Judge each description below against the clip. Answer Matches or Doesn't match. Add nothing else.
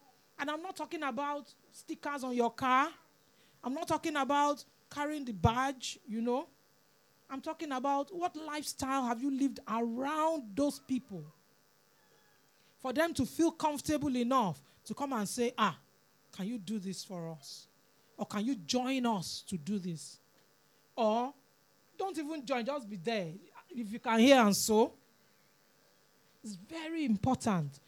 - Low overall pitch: Doesn't match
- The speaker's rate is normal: Matches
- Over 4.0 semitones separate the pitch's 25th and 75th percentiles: Matches